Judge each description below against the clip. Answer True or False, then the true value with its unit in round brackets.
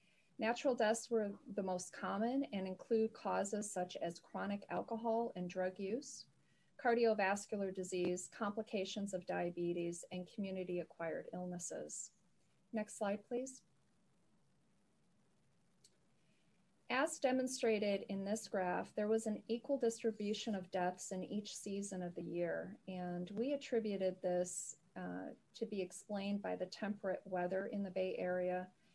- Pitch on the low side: False (200 Hz)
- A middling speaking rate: False (130 wpm)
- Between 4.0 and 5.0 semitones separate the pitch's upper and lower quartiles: False (3.4 semitones)